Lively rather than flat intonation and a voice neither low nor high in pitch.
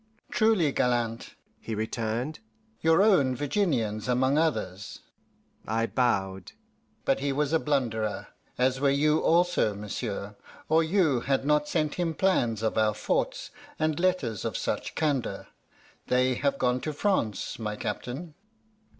No: wide, 5.7 semitones; low, 130 Hz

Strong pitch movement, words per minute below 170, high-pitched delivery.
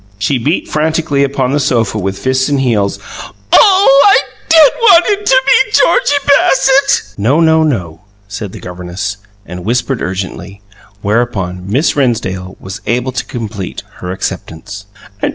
No: wide, 8.3 semitones; average, 145 wpm; low, 120 Hz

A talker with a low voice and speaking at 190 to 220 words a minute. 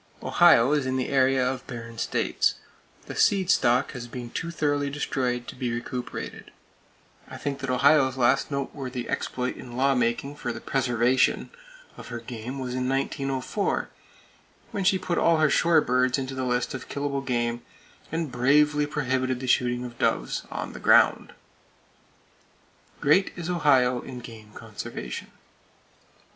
No: low, 130 Hz; average, 155 wpm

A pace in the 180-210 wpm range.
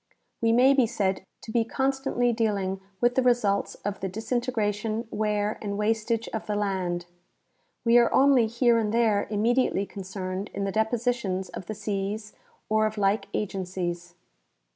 No: average, 160 wpm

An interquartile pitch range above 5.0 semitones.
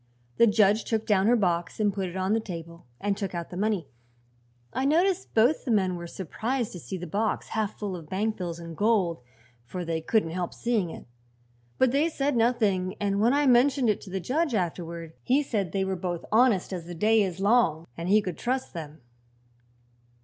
No: average, 4.7 semitones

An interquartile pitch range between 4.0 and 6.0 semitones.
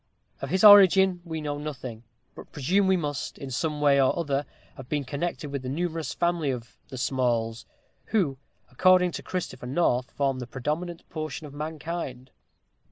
Yes: average, 4.6 semitones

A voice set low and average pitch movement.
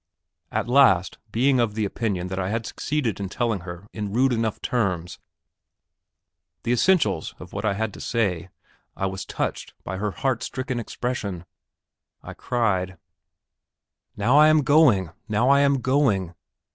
Yes: low, 110 Hz; average, 4.8 semitones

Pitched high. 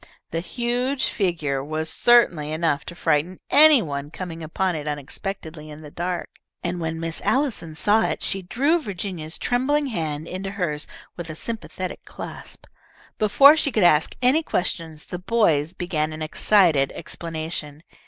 No: medium, 175 Hz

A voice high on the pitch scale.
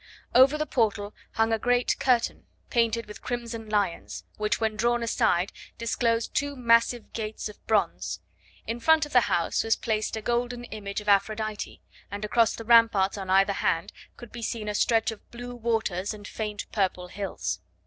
Yes: high, 225 Hz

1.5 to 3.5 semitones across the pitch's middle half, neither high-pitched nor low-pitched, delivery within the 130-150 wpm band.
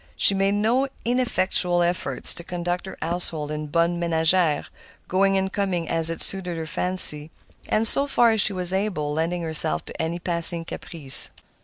No: average, 2.8 semitones; medium, 175 Hz; average, 170 wpm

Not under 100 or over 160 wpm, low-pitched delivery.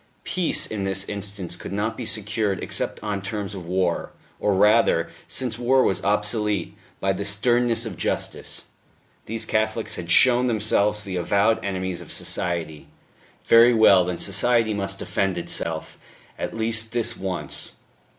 Yes: average, 150 wpm; low, 105 Hz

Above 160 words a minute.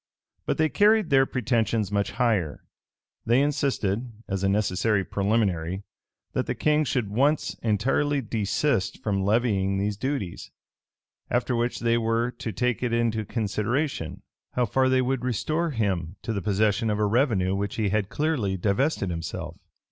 No: average, 155 wpm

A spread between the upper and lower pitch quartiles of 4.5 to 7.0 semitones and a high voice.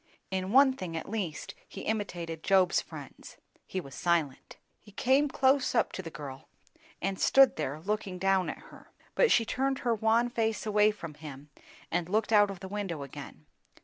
Yes: average, 5.1 semitones; high, 195 Hz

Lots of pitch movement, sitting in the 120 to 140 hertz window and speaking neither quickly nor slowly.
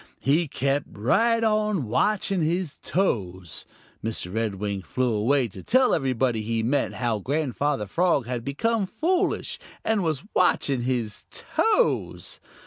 No: wide, 8.4 semitones; low, 135 Hz; slow, 130 wpm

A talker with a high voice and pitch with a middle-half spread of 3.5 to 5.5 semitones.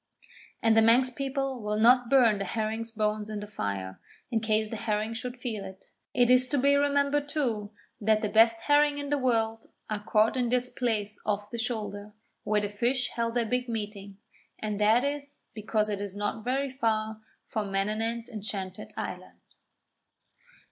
No: high, 225 Hz; average, 3.0 semitones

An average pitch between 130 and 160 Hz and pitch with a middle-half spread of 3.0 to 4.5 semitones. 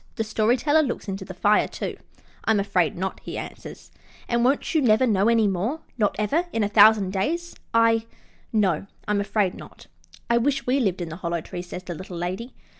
No: high, 210 Hz; average, 4.0 semitones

